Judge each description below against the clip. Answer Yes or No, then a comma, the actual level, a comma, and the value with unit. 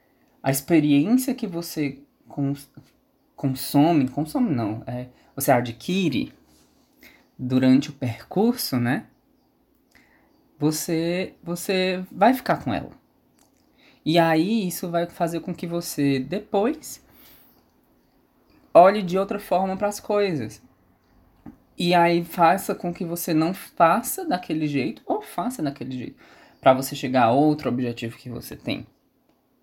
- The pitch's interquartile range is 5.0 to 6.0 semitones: Yes, wide, 5.4 semitones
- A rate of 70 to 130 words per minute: Yes, slow, 120 wpm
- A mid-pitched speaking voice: Yes, medium, 160 Hz